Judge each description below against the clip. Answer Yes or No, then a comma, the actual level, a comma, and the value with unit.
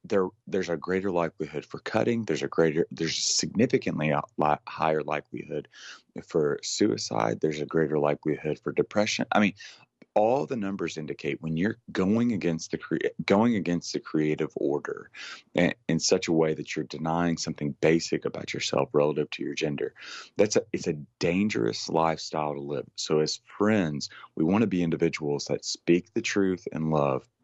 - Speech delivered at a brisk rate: No, average, 175 wpm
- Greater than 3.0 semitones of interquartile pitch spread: No, narrow, 2.5 semitones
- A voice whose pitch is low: Yes, very low, 80 Hz